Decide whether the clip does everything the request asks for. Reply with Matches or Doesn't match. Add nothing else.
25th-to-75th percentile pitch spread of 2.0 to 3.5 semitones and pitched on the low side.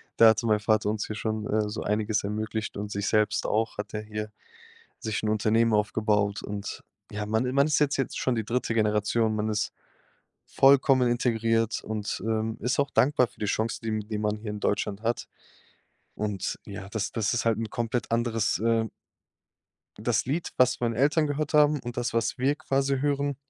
Matches